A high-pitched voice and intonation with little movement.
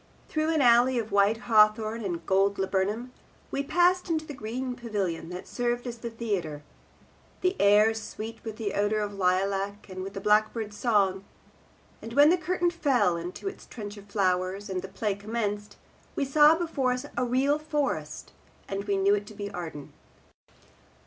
No: high, 215 Hz; average, 4.1 semitones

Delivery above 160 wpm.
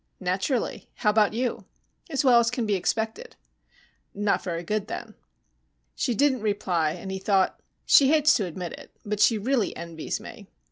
Yes: average, 170 wpm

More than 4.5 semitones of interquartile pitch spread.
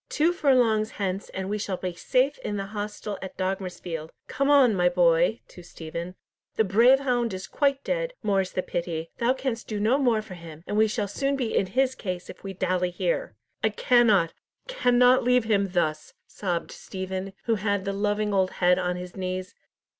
Yes: average, 4.9 semitones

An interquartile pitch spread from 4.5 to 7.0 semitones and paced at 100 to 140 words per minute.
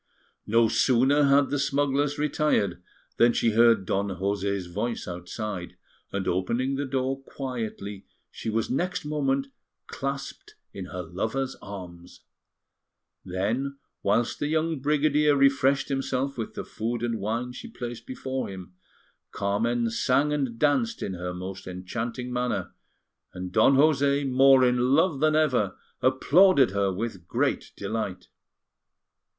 Yes: wide, 5.6 semitones; slow, 135 wpm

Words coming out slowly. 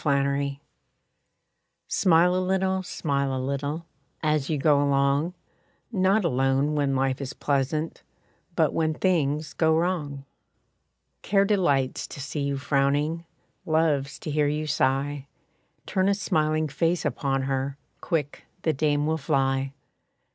Yes: slow, 130 wpm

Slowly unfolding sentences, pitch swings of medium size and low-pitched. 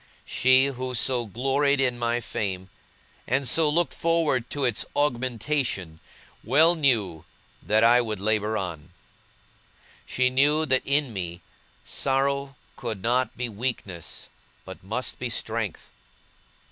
Yes: slow, 125 wpm; average, 4.1 semitones; low, 125 Hz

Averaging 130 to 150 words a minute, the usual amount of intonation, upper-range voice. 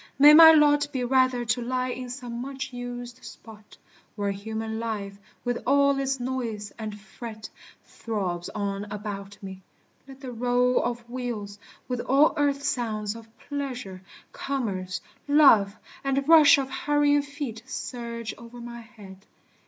Yes: average, 145 wpm; average, 4.1 semitones; high, 240 Hz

